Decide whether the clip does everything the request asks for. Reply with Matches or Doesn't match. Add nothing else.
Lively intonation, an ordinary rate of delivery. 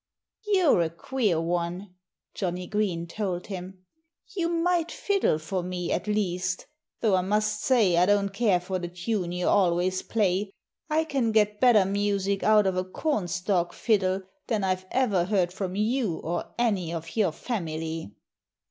Doesn't match